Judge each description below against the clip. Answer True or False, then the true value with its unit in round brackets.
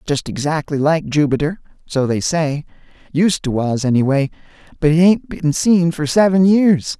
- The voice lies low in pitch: False (155 Hz)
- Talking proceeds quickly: False (155 wpm)